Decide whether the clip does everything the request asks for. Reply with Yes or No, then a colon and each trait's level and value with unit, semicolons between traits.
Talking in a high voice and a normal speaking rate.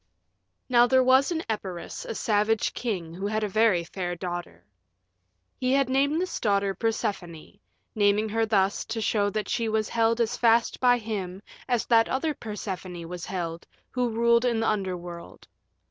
Yes: high, 215 Hz; average, 165 wpm